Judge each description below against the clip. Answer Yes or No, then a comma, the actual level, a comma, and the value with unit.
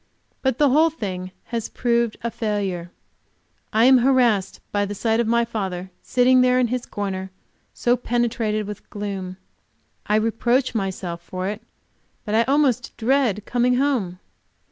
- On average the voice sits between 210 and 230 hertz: Yes, high, 225 Hz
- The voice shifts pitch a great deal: No, average, 3.8 semitones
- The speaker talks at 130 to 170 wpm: Yes, average, 150 wpm